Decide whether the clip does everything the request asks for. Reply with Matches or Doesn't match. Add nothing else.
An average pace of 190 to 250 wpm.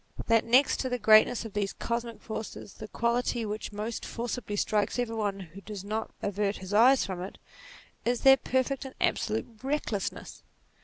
Doesn't match